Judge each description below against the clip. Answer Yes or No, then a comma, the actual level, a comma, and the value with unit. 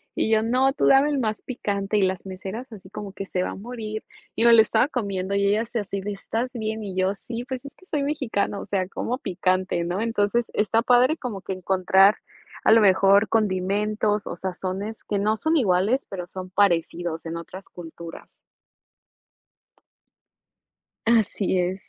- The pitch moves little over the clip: No, average, 3.4 semitones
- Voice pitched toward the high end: Yes, high, 205 Hz